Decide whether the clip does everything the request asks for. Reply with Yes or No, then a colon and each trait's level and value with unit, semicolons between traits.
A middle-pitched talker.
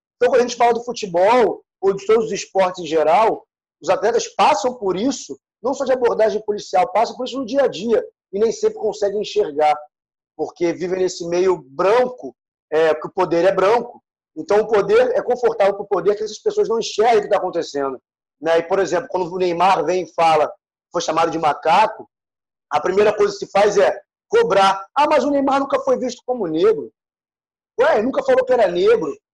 No: high, 210 Hz